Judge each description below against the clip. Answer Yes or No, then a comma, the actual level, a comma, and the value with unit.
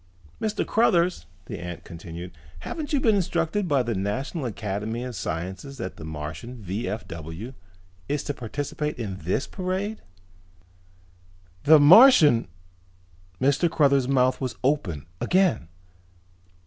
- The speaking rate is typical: No, slow, 120 wpm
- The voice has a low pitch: Yes, low, 125 Hz